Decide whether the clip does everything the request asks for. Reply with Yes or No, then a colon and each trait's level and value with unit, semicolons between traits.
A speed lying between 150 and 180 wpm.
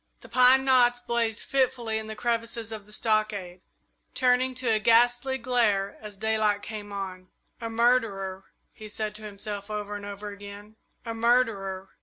Yes: average, 160 wpm